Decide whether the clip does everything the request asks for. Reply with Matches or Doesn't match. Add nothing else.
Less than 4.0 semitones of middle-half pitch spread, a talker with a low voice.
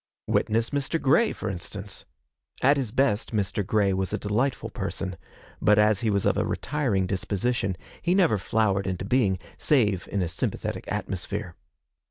Doesn't match